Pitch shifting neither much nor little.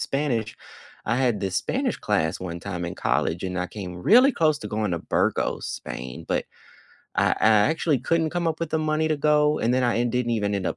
No: wide, 8.1 semitones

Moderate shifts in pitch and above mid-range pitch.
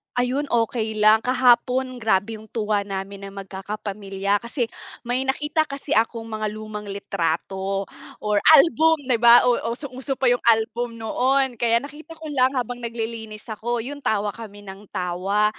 Yes: average, 3.5 semitones; high, 230 Hz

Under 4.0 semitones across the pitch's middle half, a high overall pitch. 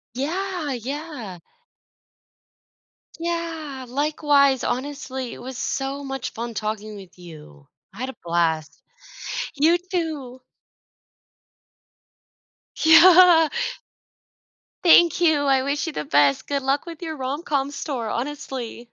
No: average, 4.8 semitones; very high, 275 Hz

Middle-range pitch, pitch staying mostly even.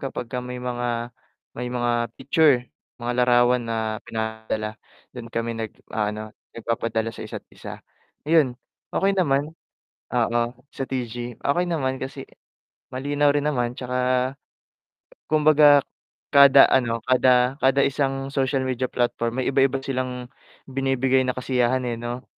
No: low, 125 Hz; narrow, 2.2 semitones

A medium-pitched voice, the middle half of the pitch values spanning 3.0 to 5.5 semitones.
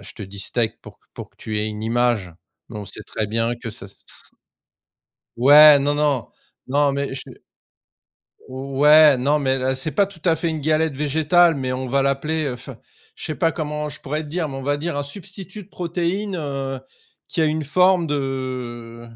Yes: medium, 145 Hz; average, 3.6 semitones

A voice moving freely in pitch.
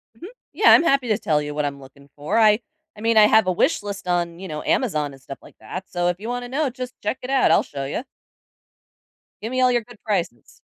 Yes: wide, 8.3 semitones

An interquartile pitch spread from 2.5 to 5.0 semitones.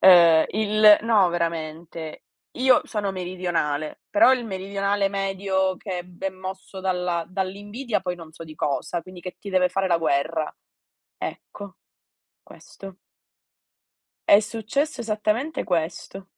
Yes: average, 2.9 semitones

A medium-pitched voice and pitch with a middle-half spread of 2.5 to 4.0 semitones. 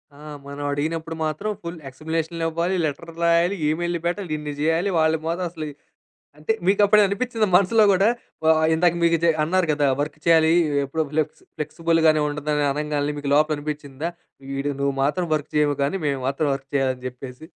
Yes: medium, 160 Hz; average, 2.8 semitones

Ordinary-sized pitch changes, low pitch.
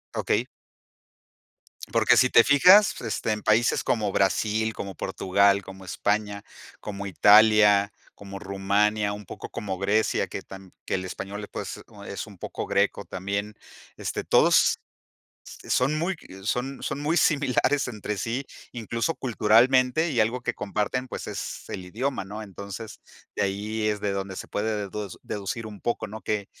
Yes: average, 3.0 semitones; low, 105 Hz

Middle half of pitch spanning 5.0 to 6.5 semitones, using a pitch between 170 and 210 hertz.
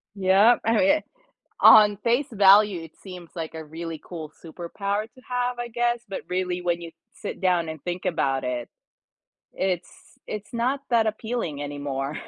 Yes: average, 5.3 semitones; medium, 185 Hz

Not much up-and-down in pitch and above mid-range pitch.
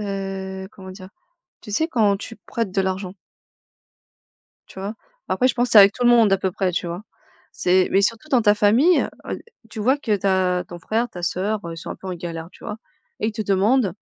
No: average, 3.0 semitones; high, 200 Hz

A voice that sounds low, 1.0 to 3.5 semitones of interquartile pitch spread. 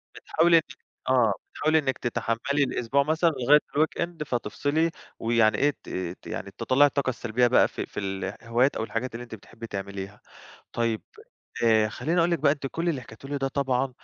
No: low, 130 Hz; average, 4.2 semitones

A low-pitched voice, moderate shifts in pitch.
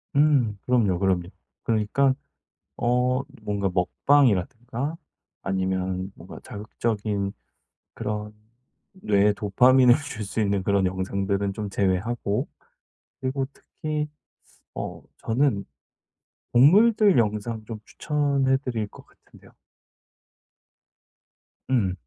Yes: low, 110 Hz; average, 4.9 semitones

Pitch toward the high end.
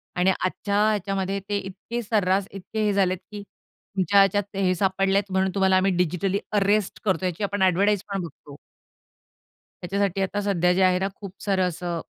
Yes: high, 195 Hz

